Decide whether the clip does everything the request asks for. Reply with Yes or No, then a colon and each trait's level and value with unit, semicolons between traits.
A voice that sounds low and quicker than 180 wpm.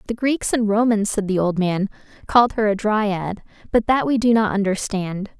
No: high, 210 Hz; average, 200 wpm